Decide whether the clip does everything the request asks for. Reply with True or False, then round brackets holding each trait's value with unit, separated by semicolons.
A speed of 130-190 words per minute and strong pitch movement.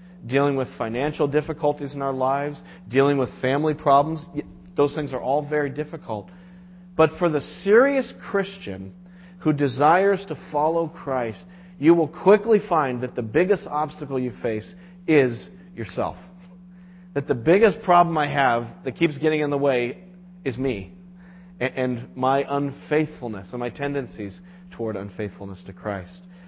True (145 wpm; 5.8 semitones)